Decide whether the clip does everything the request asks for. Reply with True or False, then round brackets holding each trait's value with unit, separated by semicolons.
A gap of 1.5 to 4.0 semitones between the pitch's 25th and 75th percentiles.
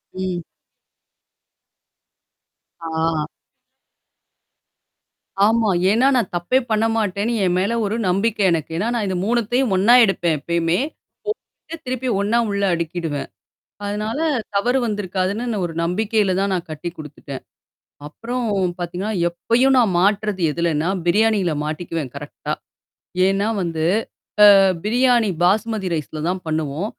False (4.6 semitones)